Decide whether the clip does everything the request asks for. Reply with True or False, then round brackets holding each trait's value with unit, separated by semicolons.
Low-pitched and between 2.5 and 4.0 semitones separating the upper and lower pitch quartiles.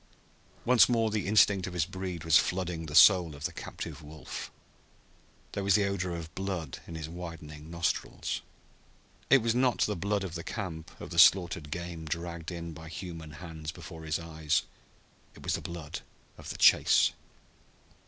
True (85 Hz; 3.1 semitones)